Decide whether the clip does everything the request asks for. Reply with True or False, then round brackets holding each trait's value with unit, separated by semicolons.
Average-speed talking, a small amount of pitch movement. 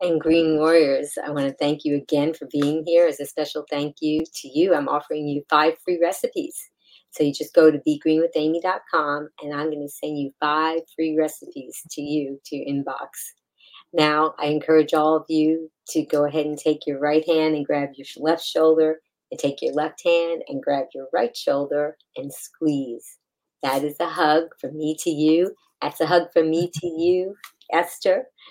True (195 wpm; 1.9 semitones)